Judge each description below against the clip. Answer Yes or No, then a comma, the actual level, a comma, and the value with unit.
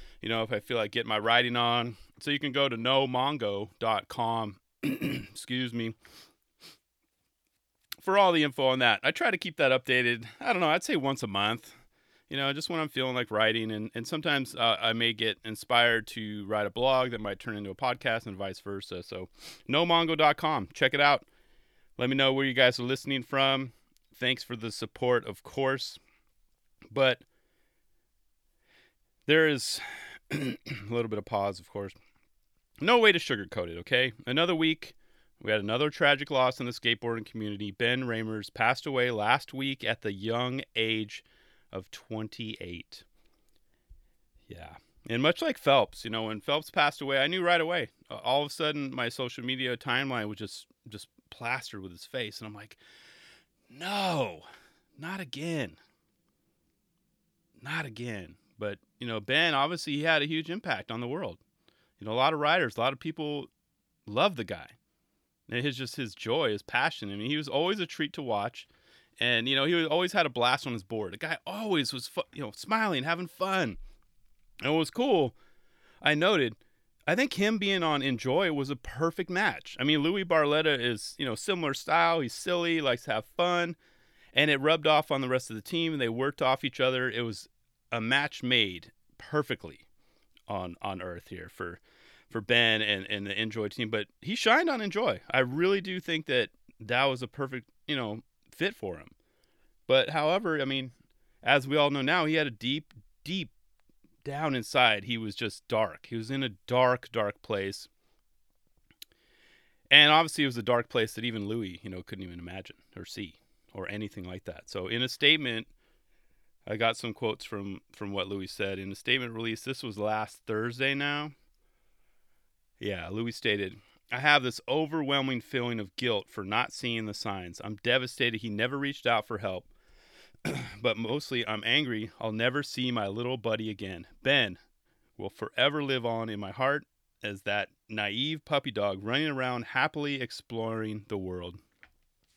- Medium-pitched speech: No, low, 125 Hz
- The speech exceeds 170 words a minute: Yes, average, 180 wpm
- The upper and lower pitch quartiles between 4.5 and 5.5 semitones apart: Yes, average, 4.8 semitones